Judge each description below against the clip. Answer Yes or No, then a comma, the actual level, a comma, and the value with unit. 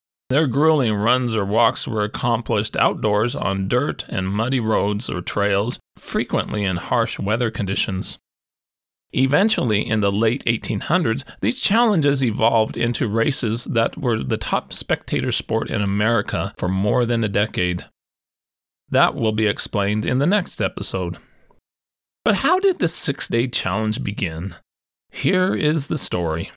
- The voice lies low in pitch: Yes, low, 115 Hz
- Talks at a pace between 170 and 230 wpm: No, average, 140 wpm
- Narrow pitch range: No, average, 4.2 semitones